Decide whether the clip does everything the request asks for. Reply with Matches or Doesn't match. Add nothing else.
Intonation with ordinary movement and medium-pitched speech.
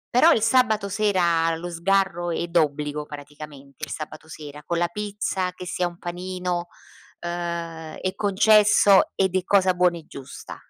Matches